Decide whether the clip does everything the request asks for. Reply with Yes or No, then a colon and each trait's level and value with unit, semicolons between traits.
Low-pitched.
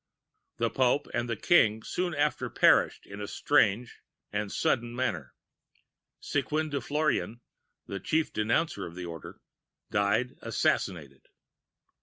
Yes: low, 115 Hz